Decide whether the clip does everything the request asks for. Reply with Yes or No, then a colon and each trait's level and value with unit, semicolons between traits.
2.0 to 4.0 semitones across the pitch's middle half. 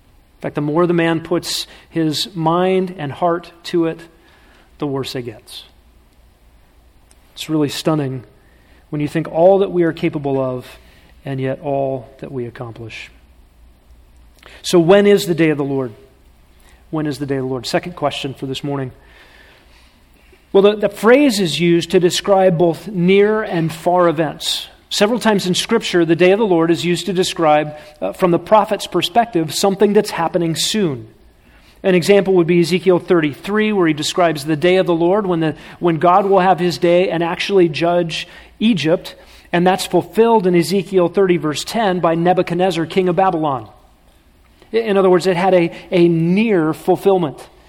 No: average, 5.1 semitones